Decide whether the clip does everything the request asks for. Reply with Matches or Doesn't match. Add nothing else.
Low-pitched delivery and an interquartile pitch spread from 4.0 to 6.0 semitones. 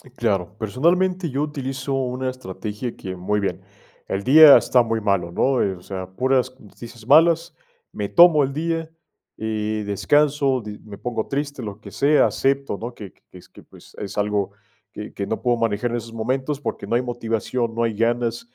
Matches